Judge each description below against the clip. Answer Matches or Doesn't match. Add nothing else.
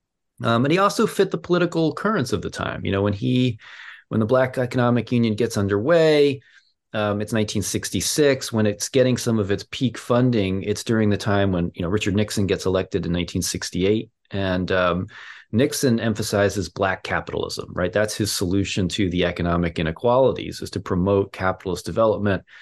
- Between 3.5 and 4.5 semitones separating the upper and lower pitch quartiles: Matches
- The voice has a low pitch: Matches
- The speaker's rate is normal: Matches